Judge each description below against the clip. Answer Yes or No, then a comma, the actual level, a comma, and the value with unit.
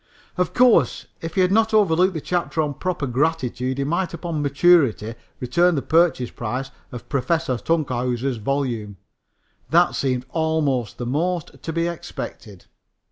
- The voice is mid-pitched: Yes, medium, 150 Hz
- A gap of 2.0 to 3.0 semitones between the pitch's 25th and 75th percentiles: No, average, 5.2 semitones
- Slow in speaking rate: No, average, 145 wpm